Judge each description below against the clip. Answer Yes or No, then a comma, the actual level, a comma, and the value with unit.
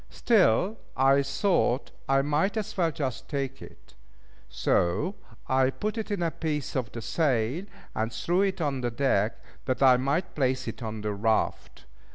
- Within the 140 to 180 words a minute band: Yes, average, 165 wpm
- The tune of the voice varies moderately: No, wide, 6.0 semitones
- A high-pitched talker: No, low, 135 Hz